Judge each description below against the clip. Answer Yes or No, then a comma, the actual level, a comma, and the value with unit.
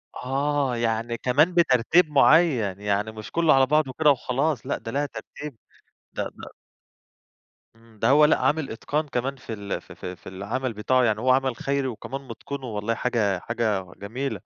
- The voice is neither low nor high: No, low, 125 Hz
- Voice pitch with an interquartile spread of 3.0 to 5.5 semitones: Yes, average, 4.2 semitones